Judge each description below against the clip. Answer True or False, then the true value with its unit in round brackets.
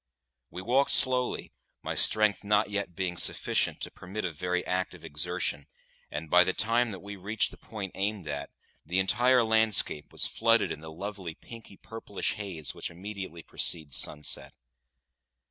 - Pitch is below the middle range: True (95 Hz)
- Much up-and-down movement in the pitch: False (3.9 semitones)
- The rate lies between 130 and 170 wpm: True (160 wpm)